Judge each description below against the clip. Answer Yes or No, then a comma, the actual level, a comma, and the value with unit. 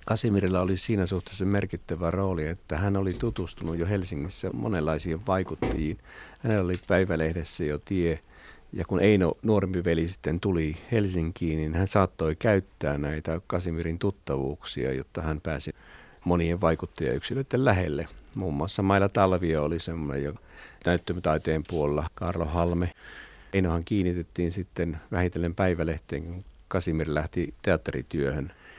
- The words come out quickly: No, average, 125 wpm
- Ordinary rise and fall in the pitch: Yes, average, 3.1 semitones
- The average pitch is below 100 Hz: Yes, very low, 85 Hz